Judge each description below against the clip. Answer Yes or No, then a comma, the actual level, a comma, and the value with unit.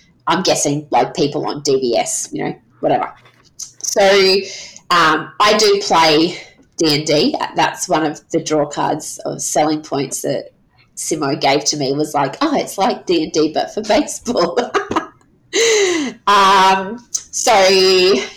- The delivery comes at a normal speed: Yes, average, 150 wpm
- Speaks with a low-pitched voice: No, high, 190 Hz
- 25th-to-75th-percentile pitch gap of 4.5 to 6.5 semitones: Yes, wide, 5.5 semitones